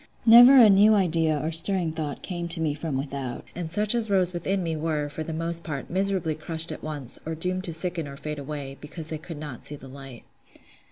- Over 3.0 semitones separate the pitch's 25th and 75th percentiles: Yes, average, 3.4 semitones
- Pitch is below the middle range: No, medium, 160 Hz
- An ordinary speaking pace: No, fast, 225 wpm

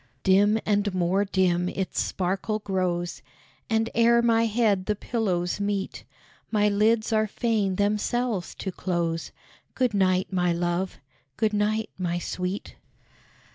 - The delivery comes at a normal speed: No, slow, 130 wpm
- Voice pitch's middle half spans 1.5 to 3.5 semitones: Yes, average, 2.9 semitones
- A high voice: Yes, high, 200 Hz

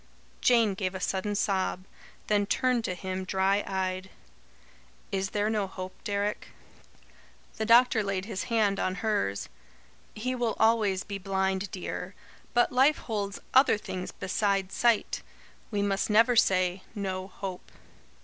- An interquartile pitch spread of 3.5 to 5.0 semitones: No, narrow, 2.6 semitones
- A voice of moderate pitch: No, high, 200 Hz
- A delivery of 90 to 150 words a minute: Yes, average, 140 wpm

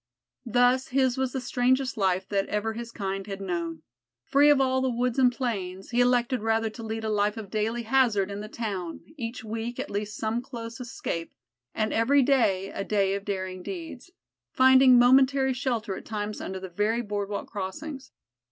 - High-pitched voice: Yes, high, 225 Hz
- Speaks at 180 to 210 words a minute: Yes, average, 185 wpm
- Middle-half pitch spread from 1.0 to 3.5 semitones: No, average, 4.1 semitones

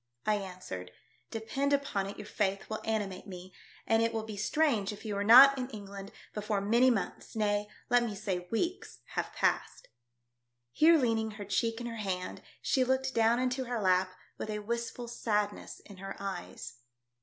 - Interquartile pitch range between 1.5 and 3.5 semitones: Yes, average, 3.2 semitones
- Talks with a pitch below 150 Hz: No, high, 215 Hz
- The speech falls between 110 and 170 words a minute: No, average, 180 wpm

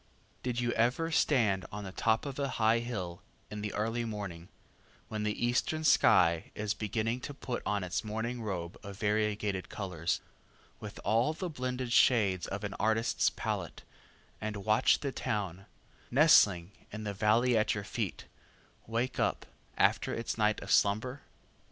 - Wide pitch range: No, average, 3.1 semitones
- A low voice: Yes, low, 110 Hz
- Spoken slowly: No, average, 155 wpm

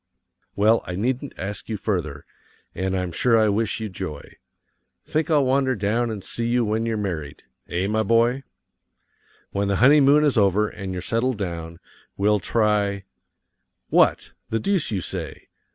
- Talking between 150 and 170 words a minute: Yes, average, 160 wpm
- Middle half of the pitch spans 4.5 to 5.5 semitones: No, average, 3.8 semitones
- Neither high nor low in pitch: No, low, 105 Hz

